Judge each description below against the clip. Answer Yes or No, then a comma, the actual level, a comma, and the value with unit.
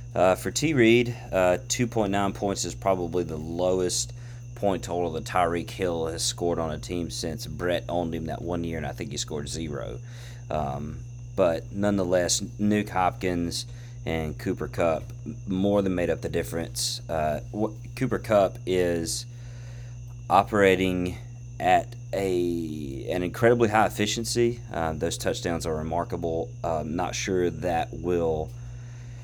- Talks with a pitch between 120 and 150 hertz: No, low, 105 Hz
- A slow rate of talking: No, average, 145 wpm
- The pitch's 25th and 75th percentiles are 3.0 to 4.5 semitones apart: No, average, 5.2 semitones